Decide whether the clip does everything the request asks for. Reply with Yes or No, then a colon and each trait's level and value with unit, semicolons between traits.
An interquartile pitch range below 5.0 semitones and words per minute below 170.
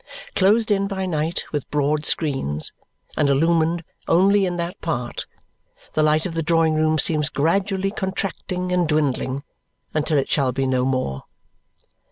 Yes: average, 3.9 semitones; average, 150 wpm